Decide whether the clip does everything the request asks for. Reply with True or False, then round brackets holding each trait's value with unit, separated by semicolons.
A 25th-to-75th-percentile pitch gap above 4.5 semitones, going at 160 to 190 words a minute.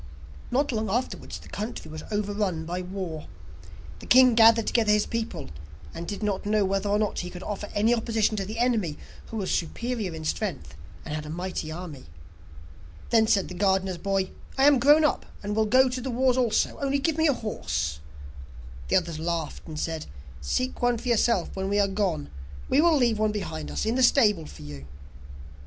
False (5.2 semitones; 200 wpm)